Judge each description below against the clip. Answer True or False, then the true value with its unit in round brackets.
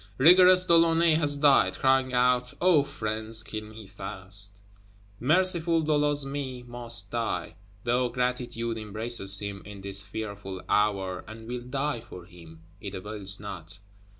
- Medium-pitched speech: False (115 Hz)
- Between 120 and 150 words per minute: True (140 wpm)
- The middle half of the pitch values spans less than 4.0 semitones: False (5.3 semitones)